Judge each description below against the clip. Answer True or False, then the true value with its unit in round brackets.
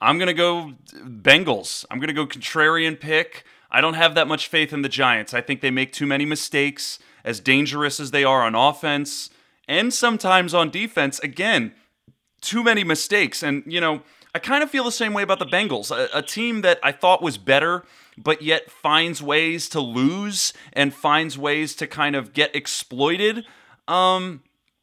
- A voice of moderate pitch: True (155 Hz)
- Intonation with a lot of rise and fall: False (4.2 semitones)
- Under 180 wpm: False (190 wpm)